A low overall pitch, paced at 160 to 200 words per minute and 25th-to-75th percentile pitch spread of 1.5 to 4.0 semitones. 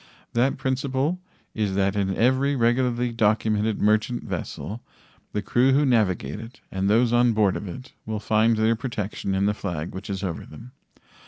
Yes: low, 110 Hz; average, 170 wpm; average, 3.5 semitones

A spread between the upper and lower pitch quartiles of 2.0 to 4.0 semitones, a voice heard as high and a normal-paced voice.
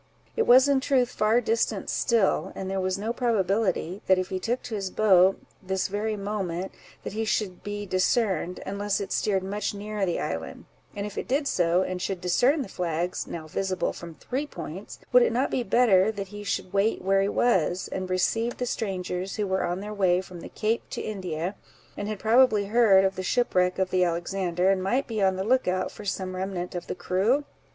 No: average, 3.0 semitones; high, 195 Hz; fast, 210 wpm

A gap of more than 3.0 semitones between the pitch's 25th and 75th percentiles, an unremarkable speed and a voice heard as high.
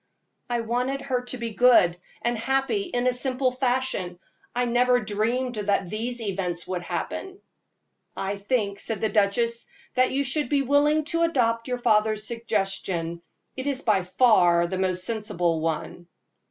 Yes: average, 4.4 semitones; average, 155 wpm; high, 230 Hz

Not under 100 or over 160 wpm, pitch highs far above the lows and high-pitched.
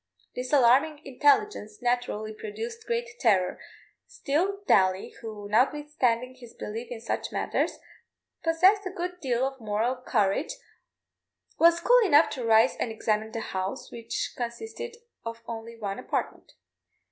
Yes: slow, 135 wpm; wide, 6.8 semitones; high, 245 Hz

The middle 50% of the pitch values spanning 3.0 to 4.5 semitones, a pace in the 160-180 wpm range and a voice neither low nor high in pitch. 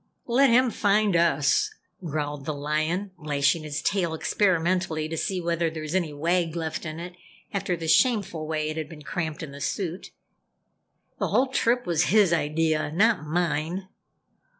Yes: average, 3.5 semitones; average, 165 wpm; medium, 165 Hz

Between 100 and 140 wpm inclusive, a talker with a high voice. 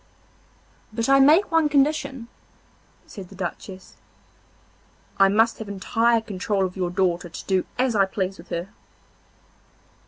Yes: slow, 135 wpm; high, 205 Hz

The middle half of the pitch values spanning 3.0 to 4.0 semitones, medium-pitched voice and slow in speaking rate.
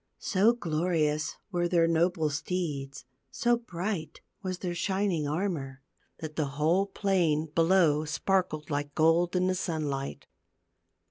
Yes: average, 3.4 semitones; medium, 165 Hz; slow, 130 wpm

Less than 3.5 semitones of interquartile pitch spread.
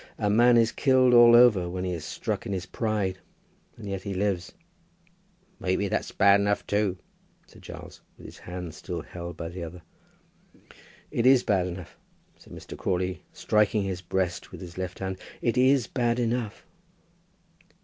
No: average, 4.3 semitones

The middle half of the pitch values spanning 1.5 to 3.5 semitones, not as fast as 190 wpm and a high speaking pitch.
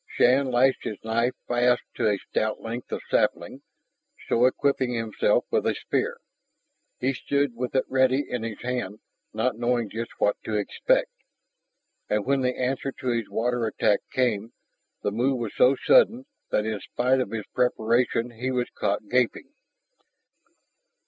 No: narrow, 2.5 semitones; average, 155 wpm; low, 120 Hz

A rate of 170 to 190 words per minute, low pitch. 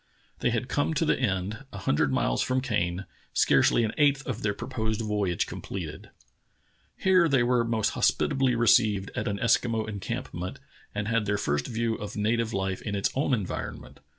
Yes: average, 180 wpm; low, 110 Hz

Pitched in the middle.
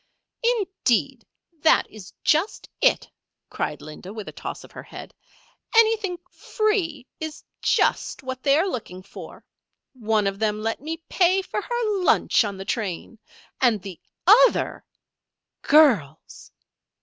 No: very high, 275 Hz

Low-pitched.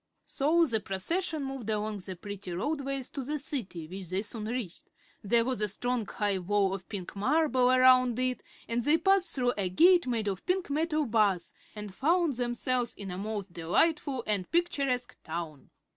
No: high, 240 Hz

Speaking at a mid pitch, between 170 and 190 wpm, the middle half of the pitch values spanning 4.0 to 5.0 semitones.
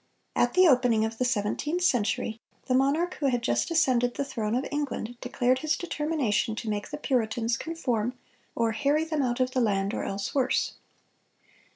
No: very high, 250 Hz; average, 180 wpm; average, 4.5 semitones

